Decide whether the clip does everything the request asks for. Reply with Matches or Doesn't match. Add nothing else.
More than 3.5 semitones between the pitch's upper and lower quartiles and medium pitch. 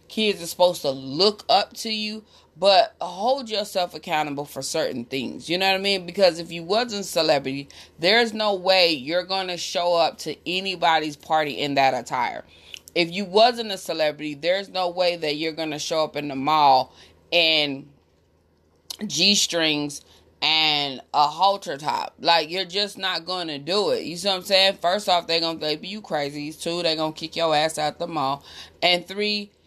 Matches